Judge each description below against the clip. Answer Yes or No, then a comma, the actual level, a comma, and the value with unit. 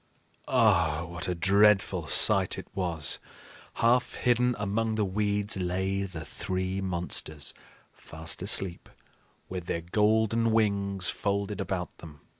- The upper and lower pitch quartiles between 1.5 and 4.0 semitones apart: Yes, average, 3.0 semitones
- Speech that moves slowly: Yes, slow, 120 wpm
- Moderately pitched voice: No, very low, 95 Hz